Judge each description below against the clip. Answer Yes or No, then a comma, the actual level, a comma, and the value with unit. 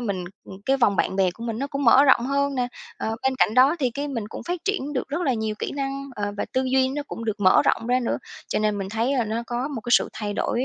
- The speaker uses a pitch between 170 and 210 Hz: No, high, 245 Hz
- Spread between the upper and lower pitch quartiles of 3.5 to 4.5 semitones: Yes, average, 4.0 semitones